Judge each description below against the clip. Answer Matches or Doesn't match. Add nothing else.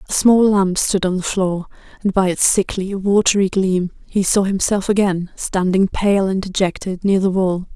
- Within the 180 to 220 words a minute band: Matches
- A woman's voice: Matches